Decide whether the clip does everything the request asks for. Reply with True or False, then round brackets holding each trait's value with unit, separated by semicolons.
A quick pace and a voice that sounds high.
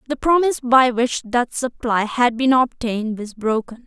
False (170 wpm; 245 Hz)